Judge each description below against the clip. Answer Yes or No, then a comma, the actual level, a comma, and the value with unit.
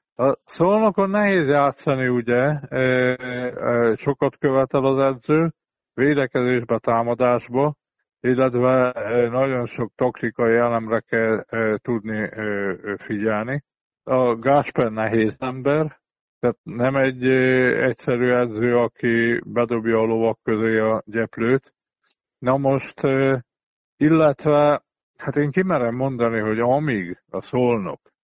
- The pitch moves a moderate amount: Yes, average, 3.0 semitones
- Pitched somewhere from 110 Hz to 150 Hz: Yes, low, 125 Hz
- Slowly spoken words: Yes, slow, 100 wpm